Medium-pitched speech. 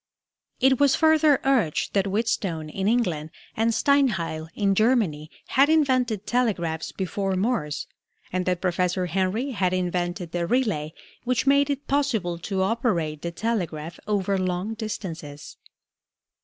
No: high, 195 Hz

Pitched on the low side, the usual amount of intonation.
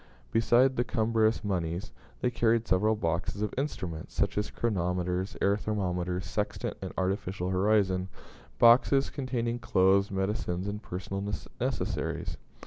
Yes: low, 100 Hz; average, 3.6 semitones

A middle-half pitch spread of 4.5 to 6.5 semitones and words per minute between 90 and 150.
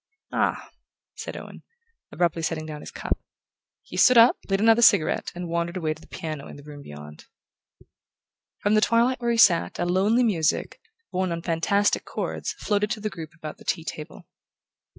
No: average, 5.2 semitones; average, 180 wpm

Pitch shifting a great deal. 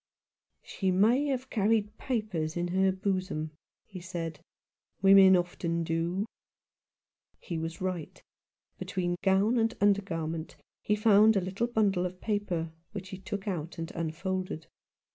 No: average, 3.3 semitones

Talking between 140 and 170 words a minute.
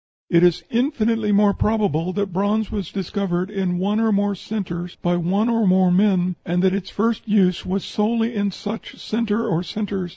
No: average, 185 wpm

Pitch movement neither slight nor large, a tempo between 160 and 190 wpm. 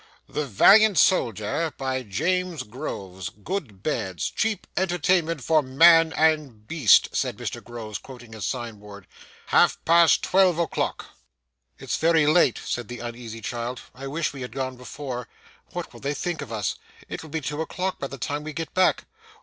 No: wide, 5.9 semitones; average, 170 wpm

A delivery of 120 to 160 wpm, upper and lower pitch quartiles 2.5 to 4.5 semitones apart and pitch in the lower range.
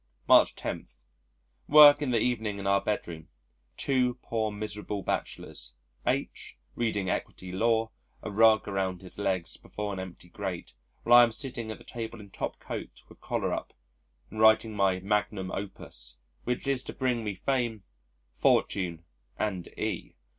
Yes: average, 155 wpm; average, 3.4 semitones; low, 105 Hz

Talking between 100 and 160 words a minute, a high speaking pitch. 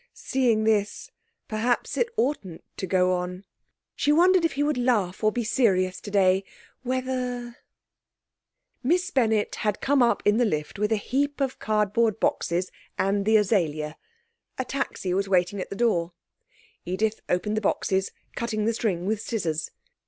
Yes: average, 155 wpm; high, 215 Hz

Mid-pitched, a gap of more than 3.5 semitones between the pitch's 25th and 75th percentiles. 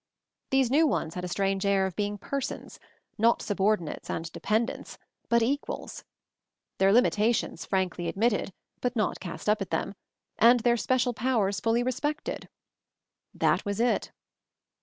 No: high, 215 Hz; average, 3.9 semitones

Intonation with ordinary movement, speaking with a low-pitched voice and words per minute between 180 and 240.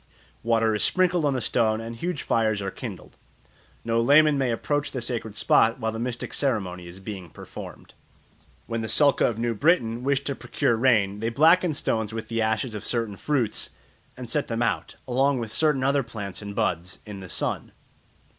Yes: average, 3.8 semitones; low, 115 Hz; average, 190 wpm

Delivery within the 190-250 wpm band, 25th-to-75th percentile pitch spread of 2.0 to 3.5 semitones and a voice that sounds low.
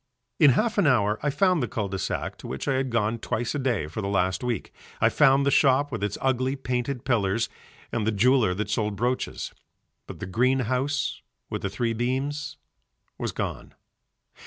No: average, 195 wpm; average, 4.1 semitones; low, 125 Hz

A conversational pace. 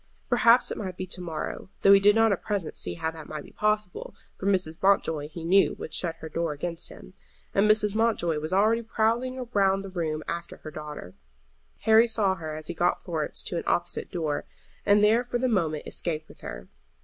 No: fast, 210 wpm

